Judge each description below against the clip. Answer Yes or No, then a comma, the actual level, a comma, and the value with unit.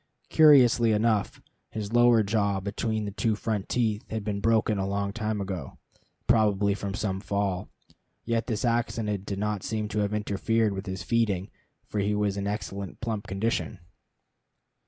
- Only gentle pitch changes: Yes, narrow, 2.0 semitones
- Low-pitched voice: Yes, low, 105 Hz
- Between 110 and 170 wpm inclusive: Yes, average, 160 wpm